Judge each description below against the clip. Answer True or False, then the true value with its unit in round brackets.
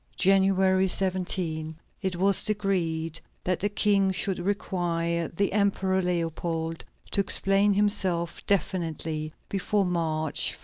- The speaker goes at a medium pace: False (115 wpm)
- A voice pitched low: False (185 Hz)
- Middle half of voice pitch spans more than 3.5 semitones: False (2.8 semitones)